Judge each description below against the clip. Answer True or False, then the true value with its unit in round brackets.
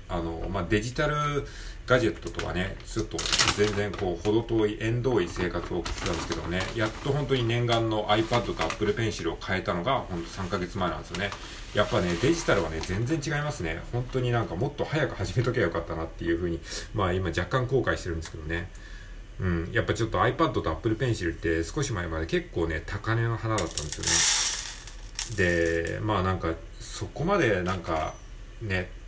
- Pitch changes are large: False (5.0 semitones)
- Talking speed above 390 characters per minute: True (425 characters per minute)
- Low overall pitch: True (100 Hz)